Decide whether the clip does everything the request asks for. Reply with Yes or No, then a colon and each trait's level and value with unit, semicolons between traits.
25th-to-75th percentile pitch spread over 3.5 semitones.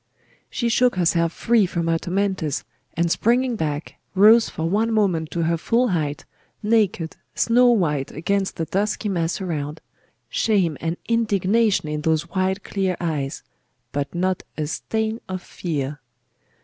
Yes: average, 4.9 semitones